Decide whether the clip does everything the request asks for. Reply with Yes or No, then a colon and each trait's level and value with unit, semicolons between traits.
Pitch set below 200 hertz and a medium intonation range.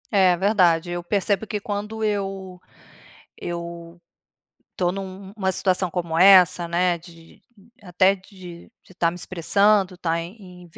No: medium, 185 Hz; narrow, 2.2 semitones